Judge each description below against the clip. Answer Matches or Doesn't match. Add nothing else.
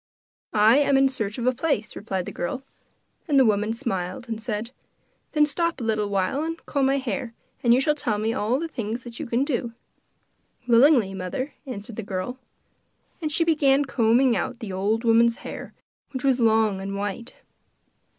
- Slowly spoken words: Doesn't match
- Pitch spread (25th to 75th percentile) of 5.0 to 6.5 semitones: Doesn't match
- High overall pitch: Matches